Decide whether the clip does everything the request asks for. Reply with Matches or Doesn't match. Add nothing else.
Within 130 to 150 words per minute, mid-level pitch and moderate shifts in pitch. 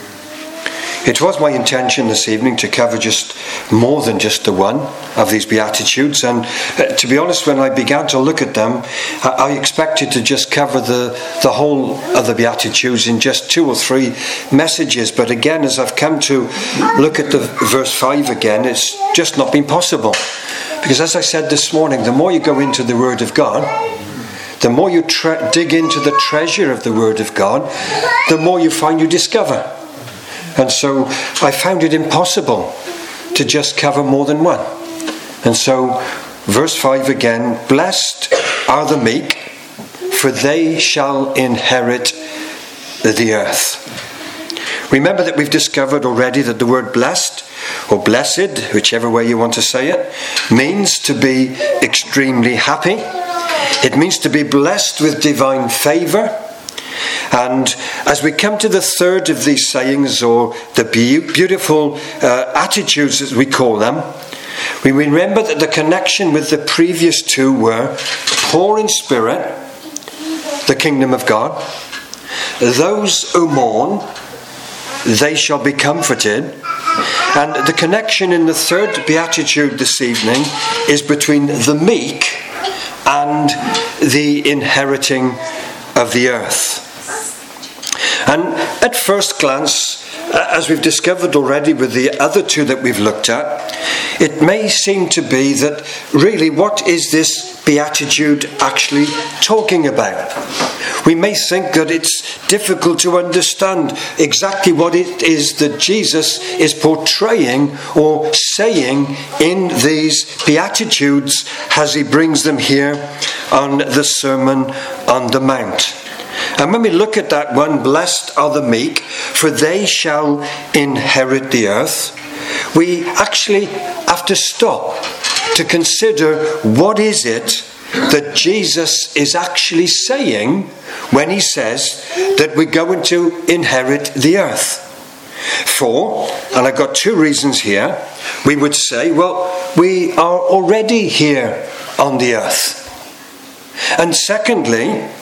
Matches